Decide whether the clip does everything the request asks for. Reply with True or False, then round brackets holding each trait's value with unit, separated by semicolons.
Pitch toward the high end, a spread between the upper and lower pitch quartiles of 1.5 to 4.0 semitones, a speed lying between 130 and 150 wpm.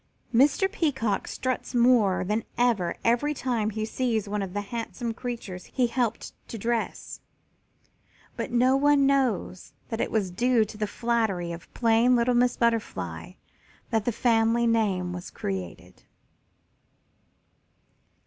True (230 Hz; 3.2 semitones; 135 wpm)